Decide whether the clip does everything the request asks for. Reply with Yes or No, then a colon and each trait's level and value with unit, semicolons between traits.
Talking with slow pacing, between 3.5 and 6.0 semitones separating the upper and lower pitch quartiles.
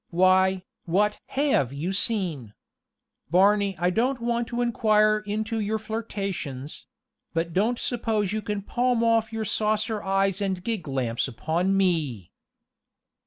Yes: slow, 130 wpm; average, 3.9 semitones